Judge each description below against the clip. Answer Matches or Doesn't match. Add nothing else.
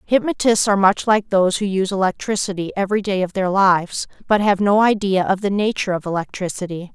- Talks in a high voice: Matches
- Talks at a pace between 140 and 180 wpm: Doesn't match